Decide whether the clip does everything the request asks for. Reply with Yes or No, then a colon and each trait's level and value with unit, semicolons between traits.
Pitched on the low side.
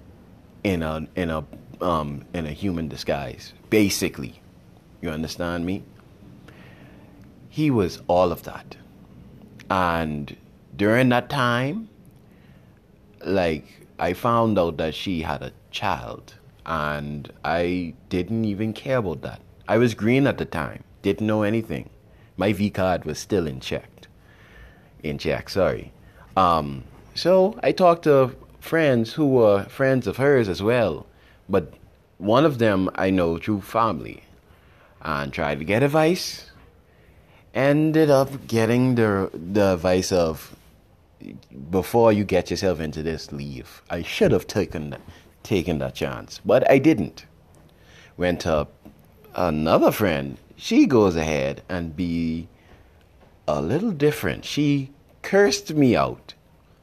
Yes: very low, 95 Hz